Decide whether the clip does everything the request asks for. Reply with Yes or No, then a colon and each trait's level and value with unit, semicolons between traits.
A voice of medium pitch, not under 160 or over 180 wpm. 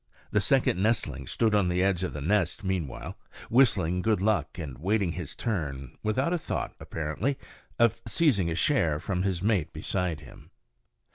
No: very low, 95 Hz; average, 165 wpm